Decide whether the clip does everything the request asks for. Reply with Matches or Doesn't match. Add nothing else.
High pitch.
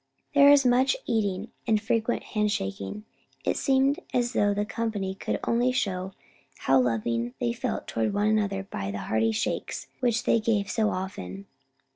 Matches